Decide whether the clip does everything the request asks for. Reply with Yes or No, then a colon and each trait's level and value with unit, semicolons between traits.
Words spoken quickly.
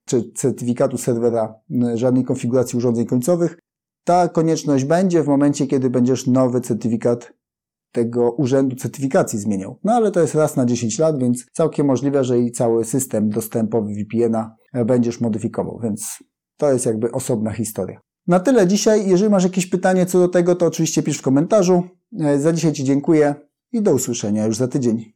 Yes: fast, 165 wpm